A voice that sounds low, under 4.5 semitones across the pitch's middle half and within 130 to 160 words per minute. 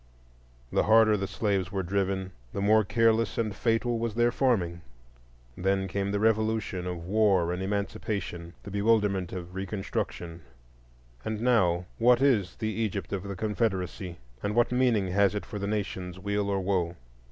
Yes: low, 100 Hz; average, 3.2 semitones; average, 155 wpm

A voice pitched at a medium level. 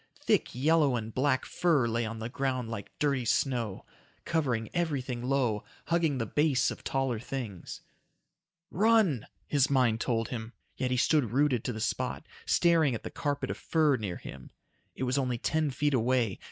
No: low, 130 Hz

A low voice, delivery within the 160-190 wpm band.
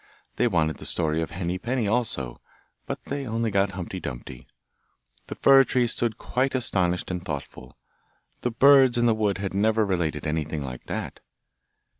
Yes: low, 100 Hz; average, 165 wpm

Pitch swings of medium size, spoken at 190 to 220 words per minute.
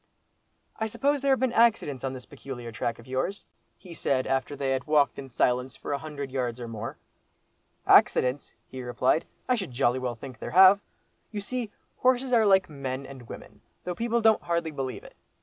No: wide, 7.9 semitones; average, 195 wpm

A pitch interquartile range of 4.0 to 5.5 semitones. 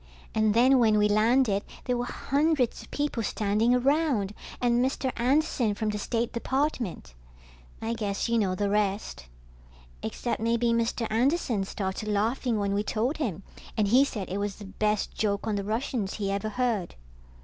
No: average, 3.4 semitones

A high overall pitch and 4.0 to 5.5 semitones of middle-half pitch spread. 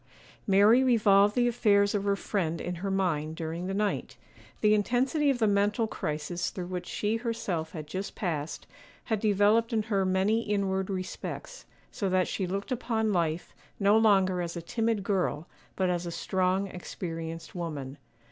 No: high, 195 Hz; average, 3.3 semitones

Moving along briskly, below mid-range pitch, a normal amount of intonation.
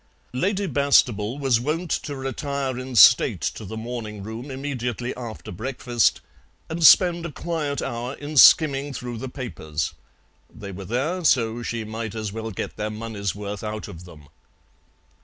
No: average, 160 wpm; low, 120 Hz; average, 4.5 semitones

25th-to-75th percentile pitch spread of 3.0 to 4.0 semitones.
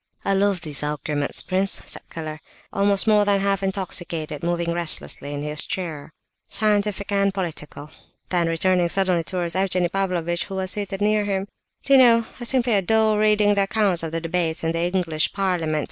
Yes: average, 3.4 semitones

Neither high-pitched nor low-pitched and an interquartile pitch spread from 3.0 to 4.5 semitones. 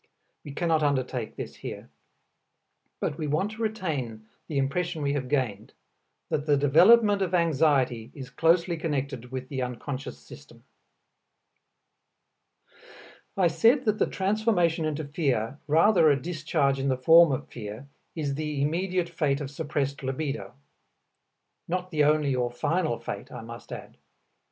Yes: medium, 150 Hz; average, 4.0 semitones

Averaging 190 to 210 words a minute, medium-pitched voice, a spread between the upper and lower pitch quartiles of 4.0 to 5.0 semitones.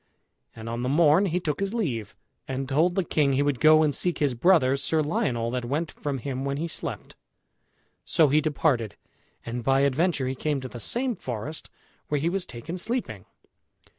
Yes: average, 195 wpm; medium, 145 Hz; average, 4.4 semitones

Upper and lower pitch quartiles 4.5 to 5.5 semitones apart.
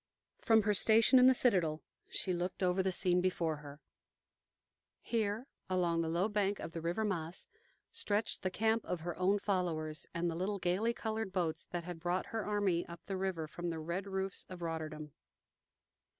No: average, 3.5 semitones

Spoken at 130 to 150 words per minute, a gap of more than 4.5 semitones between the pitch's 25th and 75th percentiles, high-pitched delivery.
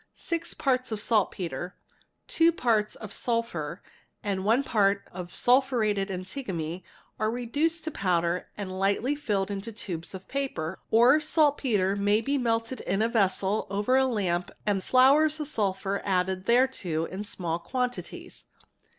Yes: average, 140 wpm; average, 5.1 semitones; high, 210 Hz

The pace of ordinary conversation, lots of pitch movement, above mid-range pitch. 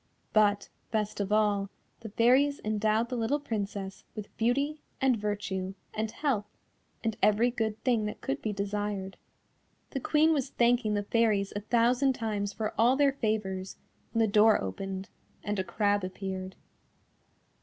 No: average, 155 wpm; average, 2.8 semitones; high, 215 Hz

